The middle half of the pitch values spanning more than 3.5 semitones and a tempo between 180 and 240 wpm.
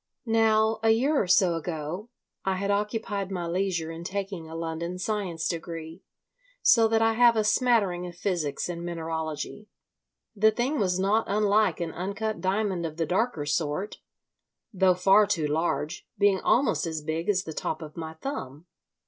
No: average, 4.4 semitones; average, 165 wpm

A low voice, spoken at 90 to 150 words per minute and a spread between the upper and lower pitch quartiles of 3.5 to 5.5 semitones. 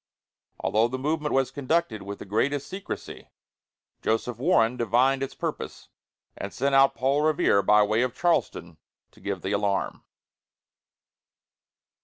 Yes: low, 125 Hz; slow, 135 wpm; average, 5.1 semitones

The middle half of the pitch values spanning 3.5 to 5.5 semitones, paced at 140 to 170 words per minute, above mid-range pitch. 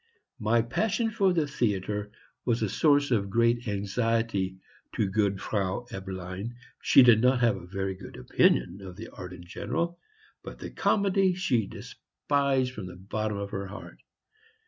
No: average, 4.6 semitones; average, 160 wpm; low, 110 Hz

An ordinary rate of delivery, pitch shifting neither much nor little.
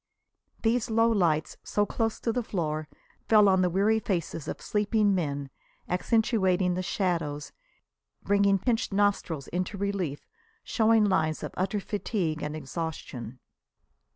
No: slow, 130 wpm; average, 4.8 semitones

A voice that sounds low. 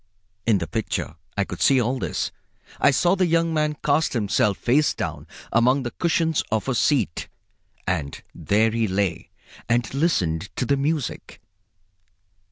Yes: low, 125 Hz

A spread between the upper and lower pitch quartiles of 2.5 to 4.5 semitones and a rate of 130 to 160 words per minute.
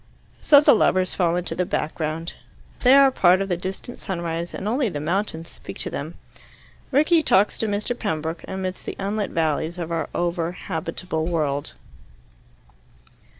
Yes: average, 3.9 semitones; average, 155 wpm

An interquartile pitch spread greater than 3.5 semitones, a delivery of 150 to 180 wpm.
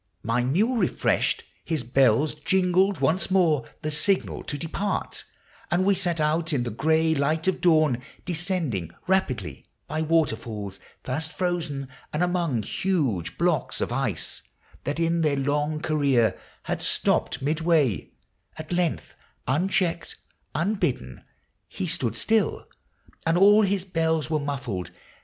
No: average, 4.5 semitones; slow, 135 wpm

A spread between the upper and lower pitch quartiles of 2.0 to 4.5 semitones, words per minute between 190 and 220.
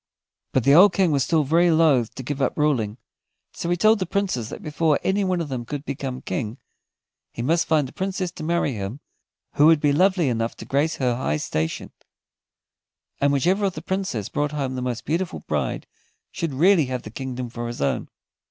No: average, 5.2 semitones; fast, 205 wpm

